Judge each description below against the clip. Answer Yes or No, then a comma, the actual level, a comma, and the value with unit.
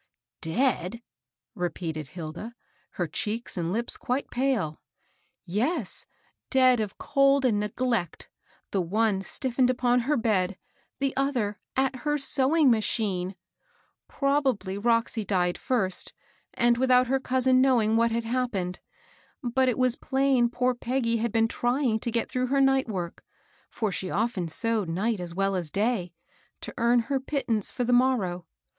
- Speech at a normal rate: Yes, average, 165 wpm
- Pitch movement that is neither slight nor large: Yes, average, 4.7 semitones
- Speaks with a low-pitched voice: No, high, 235 Hz